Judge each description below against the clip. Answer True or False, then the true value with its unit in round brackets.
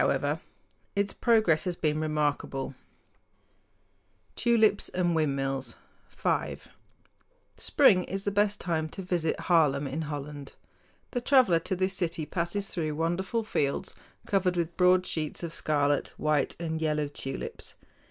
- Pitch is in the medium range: True (165 Hz)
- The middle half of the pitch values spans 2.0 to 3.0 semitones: False (3.9 semitones)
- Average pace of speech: False (125 wpm)